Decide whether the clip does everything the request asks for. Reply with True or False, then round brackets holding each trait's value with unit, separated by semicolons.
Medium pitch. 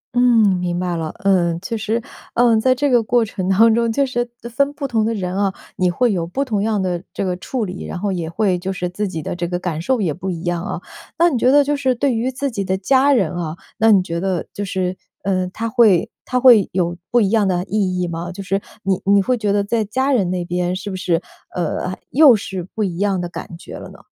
False (195 Hz)